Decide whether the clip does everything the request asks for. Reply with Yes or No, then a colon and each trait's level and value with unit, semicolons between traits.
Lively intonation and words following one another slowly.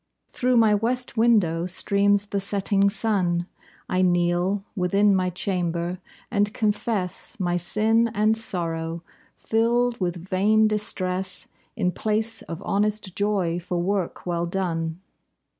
No: average, 3.2 semitones; slow, 125 wpm